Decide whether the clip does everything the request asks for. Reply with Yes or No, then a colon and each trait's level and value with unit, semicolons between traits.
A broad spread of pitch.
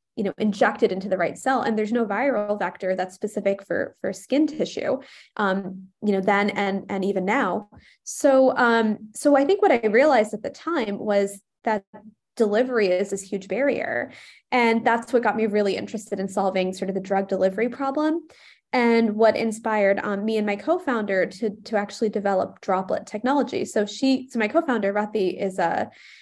No: average, 3.4 semitones